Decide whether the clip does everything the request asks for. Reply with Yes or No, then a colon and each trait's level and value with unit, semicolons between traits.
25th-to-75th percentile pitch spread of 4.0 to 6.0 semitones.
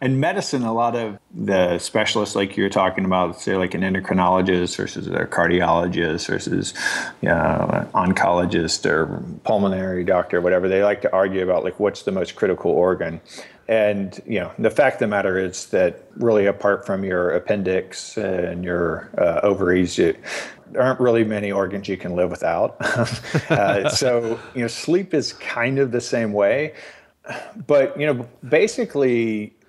Yes: average, 4.4 semitones